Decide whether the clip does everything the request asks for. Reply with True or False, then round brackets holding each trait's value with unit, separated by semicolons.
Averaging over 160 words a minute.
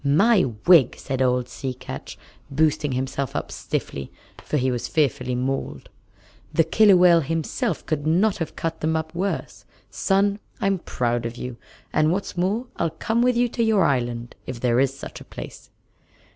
True (170 wpm)